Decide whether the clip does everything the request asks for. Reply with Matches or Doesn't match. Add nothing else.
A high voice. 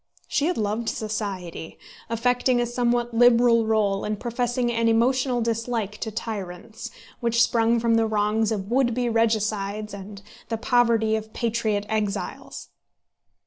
Matches